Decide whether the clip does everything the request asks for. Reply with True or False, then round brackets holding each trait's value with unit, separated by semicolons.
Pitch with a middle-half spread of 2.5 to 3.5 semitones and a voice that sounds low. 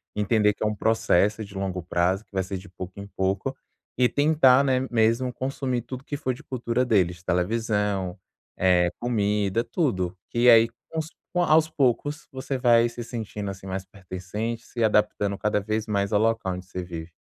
False (4.2 semitones; 105 Hz)